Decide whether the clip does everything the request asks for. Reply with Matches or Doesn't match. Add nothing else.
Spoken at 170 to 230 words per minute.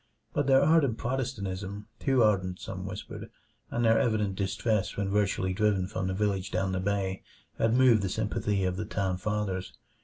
Matches